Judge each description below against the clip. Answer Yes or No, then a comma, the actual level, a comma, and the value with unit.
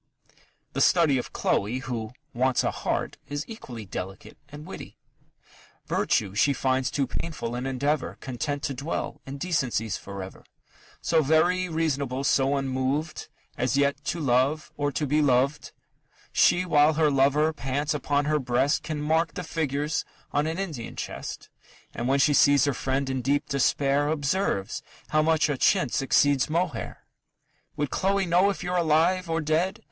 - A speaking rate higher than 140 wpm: Yes, average, 160 wpm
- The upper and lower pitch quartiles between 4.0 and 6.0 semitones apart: No, average, 3.2 semitones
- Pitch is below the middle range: No, medium, 145 Hz